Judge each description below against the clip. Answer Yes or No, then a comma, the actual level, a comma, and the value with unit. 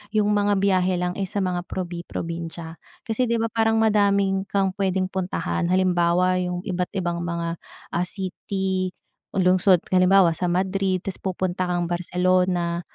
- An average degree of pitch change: No, narrow, 1.7 semitones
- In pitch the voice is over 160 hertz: Yes, medium, 185 Hz